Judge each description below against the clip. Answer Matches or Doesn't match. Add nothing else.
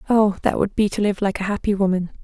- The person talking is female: Matches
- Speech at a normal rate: Doesn't match